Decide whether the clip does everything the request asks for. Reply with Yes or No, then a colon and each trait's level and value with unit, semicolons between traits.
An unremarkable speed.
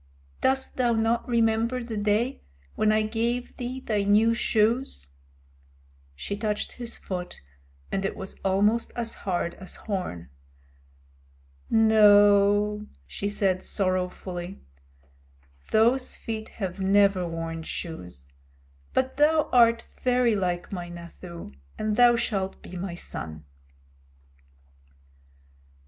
No: slow, 110 wpm